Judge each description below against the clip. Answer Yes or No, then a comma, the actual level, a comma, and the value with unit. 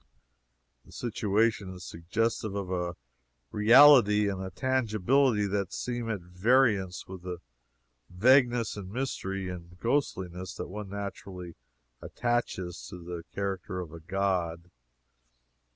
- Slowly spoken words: Yes, slow, 120 wpm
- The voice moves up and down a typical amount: Yes, average, 4.1 semitones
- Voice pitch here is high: No, low, 100 Hz